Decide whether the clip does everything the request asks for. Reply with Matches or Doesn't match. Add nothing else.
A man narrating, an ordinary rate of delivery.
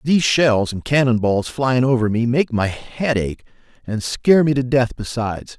Matches